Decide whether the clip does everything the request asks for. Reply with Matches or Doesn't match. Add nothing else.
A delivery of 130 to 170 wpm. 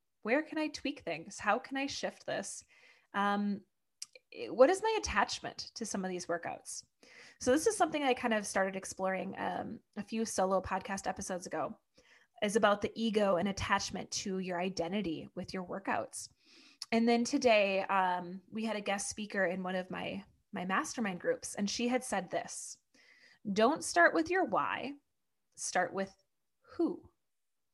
Matches